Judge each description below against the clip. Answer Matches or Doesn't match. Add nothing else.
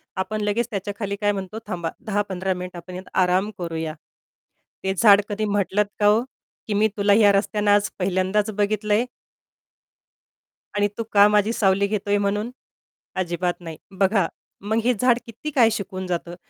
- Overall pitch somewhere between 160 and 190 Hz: Doesn't match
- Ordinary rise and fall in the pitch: Doesn't match